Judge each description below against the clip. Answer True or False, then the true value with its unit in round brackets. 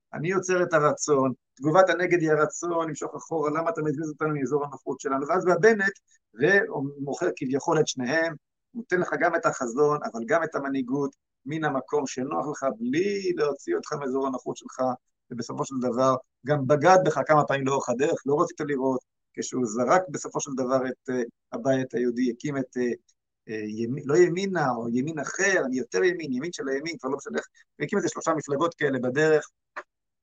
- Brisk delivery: True (170 wpm)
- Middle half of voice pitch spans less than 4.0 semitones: False (4.3 semitones)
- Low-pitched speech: False (150 Hz)